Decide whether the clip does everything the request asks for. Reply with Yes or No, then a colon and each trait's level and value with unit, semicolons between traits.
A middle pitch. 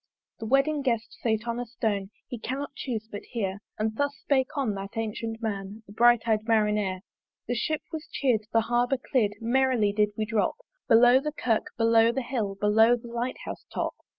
No: high, 230 Hz